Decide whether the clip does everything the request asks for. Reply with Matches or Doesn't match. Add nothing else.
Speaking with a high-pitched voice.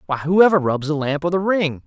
Doesn't match